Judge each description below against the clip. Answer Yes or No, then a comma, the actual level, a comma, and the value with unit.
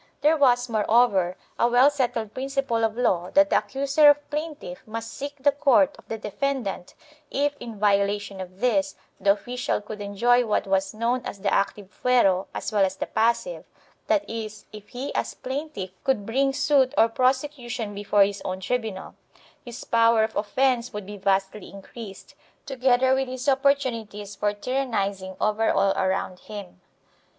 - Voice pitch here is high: Yes, high, 230 Hz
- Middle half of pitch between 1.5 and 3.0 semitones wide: No, average, 4.5 semitones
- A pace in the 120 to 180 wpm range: Yes, average, 175 wpm